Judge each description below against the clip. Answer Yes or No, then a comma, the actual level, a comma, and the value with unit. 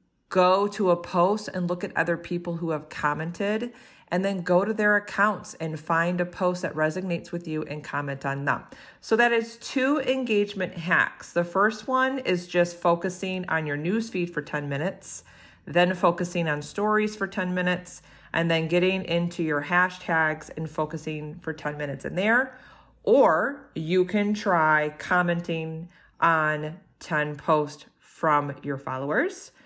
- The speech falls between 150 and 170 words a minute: Yes, average, 160 wpm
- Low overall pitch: No, medium, 175 Hz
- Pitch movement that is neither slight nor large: Yes, average, 3.7 semitones